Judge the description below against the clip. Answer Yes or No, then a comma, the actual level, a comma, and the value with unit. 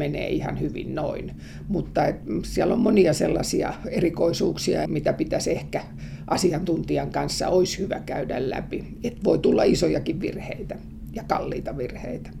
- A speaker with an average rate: Yes, average, 135 wpm